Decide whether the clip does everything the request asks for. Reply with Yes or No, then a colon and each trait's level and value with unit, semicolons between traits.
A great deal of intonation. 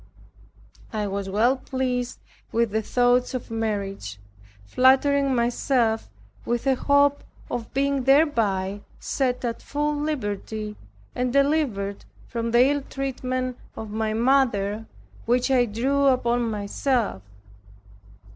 No: average, 3.7 semitones